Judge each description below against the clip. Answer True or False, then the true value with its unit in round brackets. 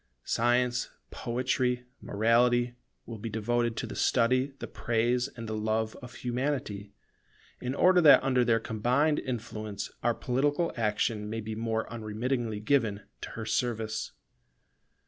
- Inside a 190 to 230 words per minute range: False (135 wpm)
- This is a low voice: True (120 Hz)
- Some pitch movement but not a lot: False (2.3 semitones)